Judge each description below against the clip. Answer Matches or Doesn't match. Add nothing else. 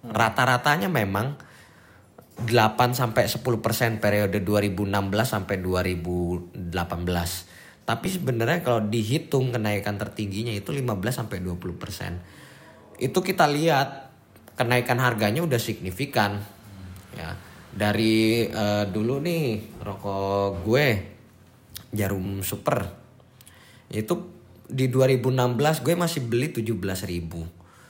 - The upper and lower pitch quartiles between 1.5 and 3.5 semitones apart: Doesn't match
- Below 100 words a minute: Matches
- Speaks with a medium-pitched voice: Doesn't match